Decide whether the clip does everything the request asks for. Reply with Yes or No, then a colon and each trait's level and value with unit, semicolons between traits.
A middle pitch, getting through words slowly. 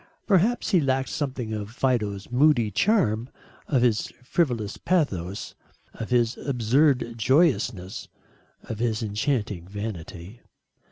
No: low, 120 Hz; slow, 110 wpm